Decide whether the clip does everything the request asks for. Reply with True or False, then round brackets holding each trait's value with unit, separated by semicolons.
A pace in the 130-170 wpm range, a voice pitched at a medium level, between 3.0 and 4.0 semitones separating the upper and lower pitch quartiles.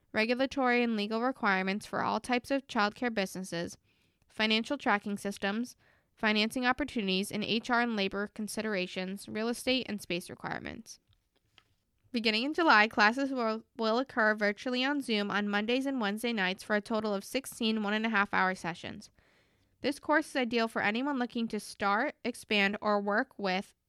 False (160 wpm; 215 Hz; 3.4 semitones)